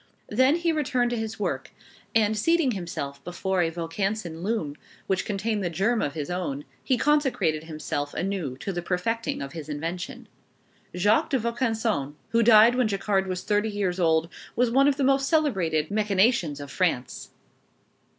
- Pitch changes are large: Yes, wide, 5.8 semitones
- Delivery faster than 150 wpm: Yes, average, 165 wpm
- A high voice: Yes, high, 195 Hz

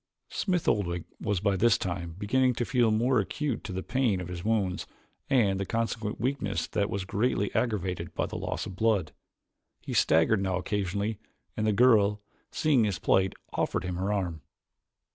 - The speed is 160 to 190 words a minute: Yes, average, 165 wpm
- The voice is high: No, low, 100 Hz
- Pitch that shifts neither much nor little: Yes, average, 3.6 semitones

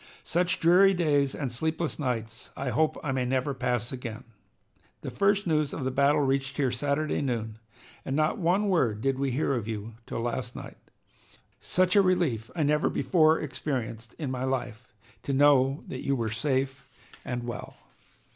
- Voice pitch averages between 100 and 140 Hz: Yes, low, 135 Hz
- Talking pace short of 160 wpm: No, average, 175 wpm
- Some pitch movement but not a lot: Yes, average, 3.9 semitones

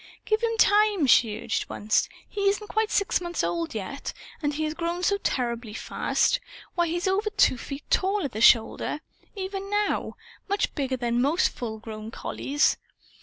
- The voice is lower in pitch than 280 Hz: No, very high, 315 Hz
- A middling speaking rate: Yes, average, 170 wpm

